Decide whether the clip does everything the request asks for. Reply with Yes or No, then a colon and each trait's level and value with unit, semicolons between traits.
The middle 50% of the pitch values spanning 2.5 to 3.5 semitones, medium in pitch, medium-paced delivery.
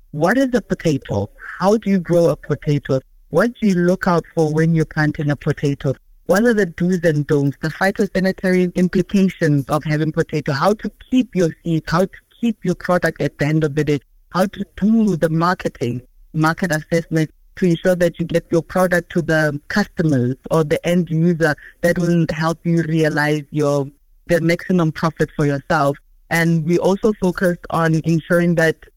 Yes: average, 3.1 semitones; medium, 165 Hz; average, 180 wpm